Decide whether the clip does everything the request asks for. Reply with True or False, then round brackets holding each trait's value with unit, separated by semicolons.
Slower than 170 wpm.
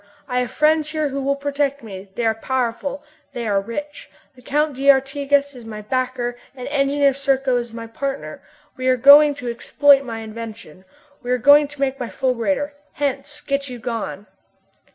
False (175 wpm)